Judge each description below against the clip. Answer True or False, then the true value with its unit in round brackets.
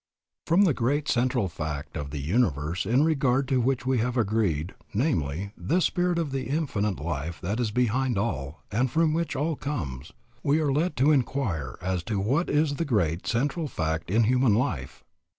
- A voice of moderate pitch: False (120 Hz)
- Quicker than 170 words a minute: True (180 wpm)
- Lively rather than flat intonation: True (8.3 semitones)